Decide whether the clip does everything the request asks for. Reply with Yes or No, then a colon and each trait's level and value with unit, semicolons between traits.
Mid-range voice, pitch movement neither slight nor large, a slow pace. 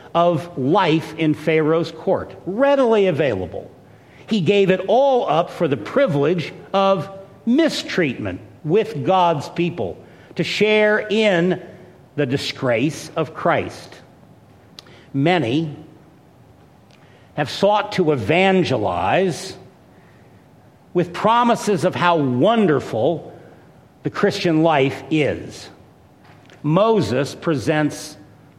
Yes: medium, 170 Hz; average, 4.8 semitones; slow, 90 wpm